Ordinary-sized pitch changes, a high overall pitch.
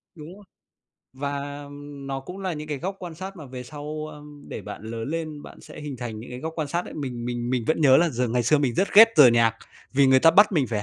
No: average, 4.1 semitones; medium, 145 Hz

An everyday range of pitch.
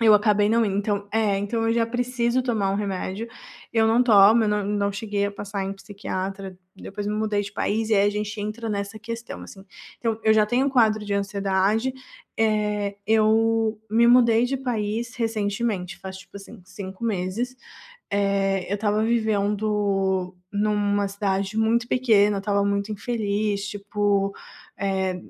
No: narrow, 2.0 semitones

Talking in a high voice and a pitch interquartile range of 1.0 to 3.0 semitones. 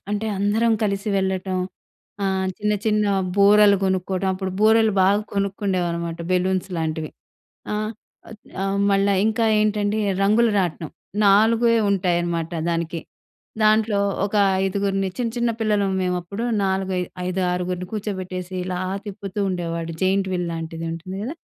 Yes: high, 195 Hz; narrow, 2.5 semitones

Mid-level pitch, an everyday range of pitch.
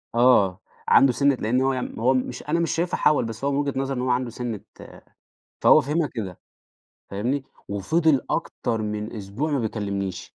No: low, 125 Hz; average, 4.7 semitones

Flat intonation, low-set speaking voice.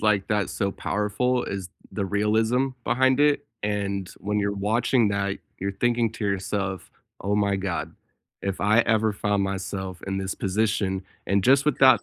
Yes: narrow, 2.3 semitones; low, 100 Hz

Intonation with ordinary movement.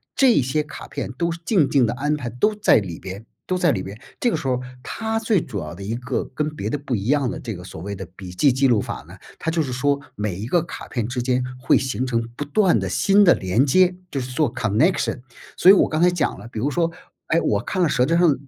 No: wide, 6.4 semitones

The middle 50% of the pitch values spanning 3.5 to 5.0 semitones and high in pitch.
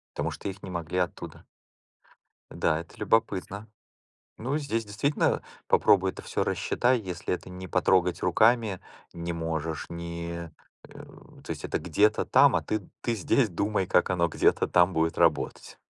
No: average, 4.0 semitones; very low, 90 Hz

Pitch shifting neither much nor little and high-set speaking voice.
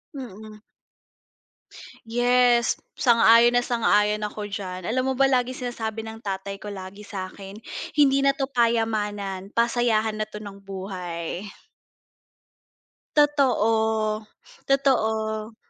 Yes: average, 3.0 semitones; high, 220 Hz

